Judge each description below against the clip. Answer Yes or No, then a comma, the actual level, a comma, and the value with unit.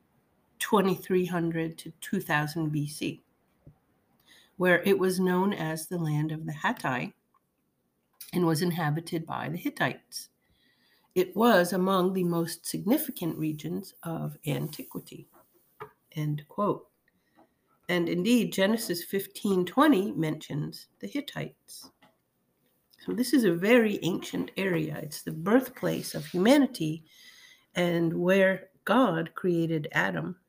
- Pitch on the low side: No, medium, 180 Hz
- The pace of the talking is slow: Yes, slow, 110 wpm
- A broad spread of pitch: No, average, 3.3 semitones